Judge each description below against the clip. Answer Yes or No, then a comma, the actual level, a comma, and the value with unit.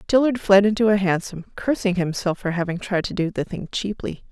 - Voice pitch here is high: Yes, high, 195 Hz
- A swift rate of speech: Yes, fast, 210 wpm